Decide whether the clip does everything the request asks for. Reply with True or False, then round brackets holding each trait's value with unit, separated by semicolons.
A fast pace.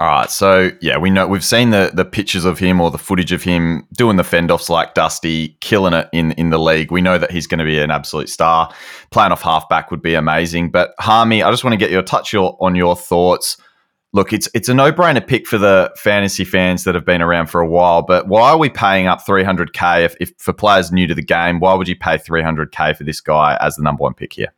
True (265 wpm)